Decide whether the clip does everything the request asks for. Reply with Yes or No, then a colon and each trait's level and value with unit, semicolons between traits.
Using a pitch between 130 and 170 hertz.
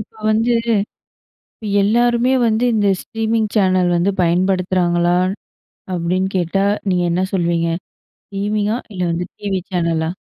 No: high, 190 Hz